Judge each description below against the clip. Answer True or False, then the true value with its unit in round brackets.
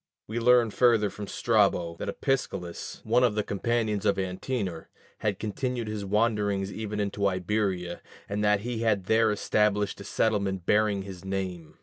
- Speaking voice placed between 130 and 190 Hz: False (105 Hz)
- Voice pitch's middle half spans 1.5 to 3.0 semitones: True (2.4 semitones)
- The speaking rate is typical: True (155 wpm)